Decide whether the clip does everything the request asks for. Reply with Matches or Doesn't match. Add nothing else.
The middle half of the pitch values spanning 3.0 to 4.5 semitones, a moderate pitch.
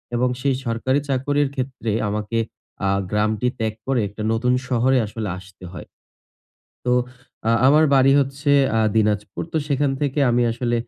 Doesn't match